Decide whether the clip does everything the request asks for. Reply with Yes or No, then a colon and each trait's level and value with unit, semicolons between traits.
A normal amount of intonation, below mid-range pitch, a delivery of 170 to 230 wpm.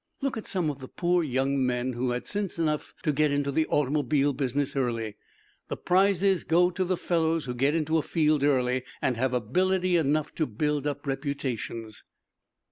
No: average, 4.3 semitones; medium, 145 Hz; average, 185 wpm